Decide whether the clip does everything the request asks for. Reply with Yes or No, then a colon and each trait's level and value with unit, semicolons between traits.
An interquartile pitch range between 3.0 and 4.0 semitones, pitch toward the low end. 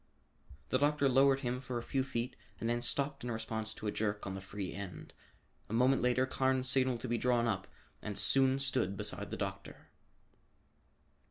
Yes: average, 3.3 semitones; low, 125 Hz